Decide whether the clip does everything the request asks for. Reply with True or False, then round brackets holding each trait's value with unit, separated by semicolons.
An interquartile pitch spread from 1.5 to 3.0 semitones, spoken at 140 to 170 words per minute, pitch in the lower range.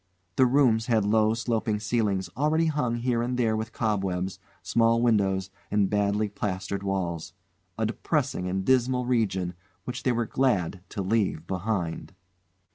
False (3.7 semitones; 145 wpm; 110 Hz)